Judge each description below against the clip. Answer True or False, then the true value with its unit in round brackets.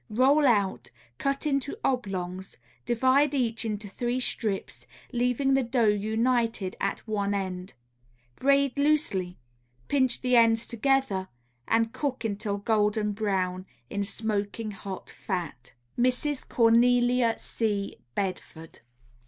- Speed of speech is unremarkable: False (110 wpm)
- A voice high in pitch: True (225 Hz)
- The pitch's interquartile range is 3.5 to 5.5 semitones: True (4.1 semitones)